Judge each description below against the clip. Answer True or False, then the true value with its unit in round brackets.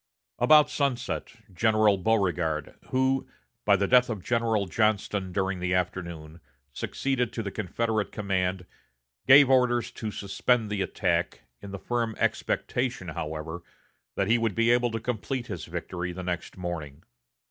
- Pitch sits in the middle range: False (105 Hz)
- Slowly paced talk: False (145 wpm)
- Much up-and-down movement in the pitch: False (4.8 semitones)